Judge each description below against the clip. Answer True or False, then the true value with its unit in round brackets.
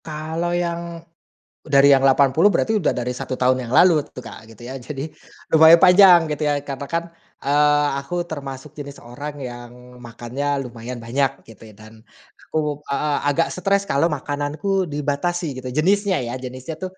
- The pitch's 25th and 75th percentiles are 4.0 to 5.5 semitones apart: True (4.4 semitones)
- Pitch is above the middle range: False (145 Hz)